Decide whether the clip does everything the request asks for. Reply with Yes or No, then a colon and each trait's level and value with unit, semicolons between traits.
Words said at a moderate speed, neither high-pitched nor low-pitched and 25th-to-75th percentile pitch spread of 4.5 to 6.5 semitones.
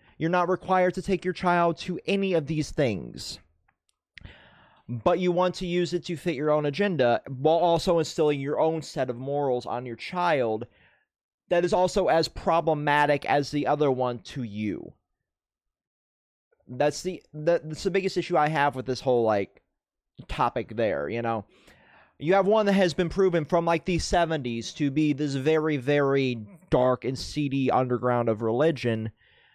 Yes: average, 170 wpm; medium, 150 Hz; wide, 5.6 semitones